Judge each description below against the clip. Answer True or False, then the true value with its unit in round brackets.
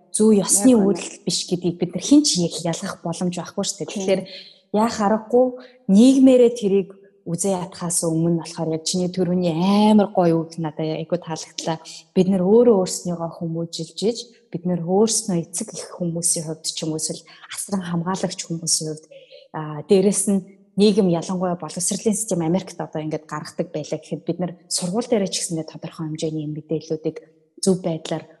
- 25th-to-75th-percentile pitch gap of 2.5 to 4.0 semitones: True (3.3 semitones)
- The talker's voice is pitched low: False (180 Hz)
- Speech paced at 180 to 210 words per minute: False (145 wpm)